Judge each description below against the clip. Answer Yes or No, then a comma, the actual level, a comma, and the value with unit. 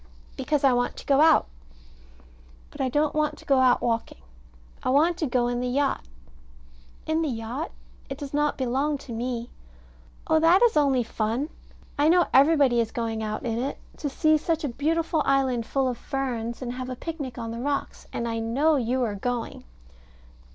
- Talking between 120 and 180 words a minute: No, average, 190 wpm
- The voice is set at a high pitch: Yes, very high, 265 Hz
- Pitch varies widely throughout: No, average, 3.8 semitones